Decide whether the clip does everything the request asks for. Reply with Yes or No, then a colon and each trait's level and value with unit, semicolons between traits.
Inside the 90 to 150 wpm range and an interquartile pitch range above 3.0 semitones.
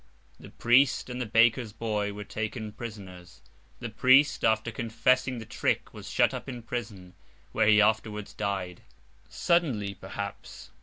No: average, 140 wpm; narrow, 2.6 semitones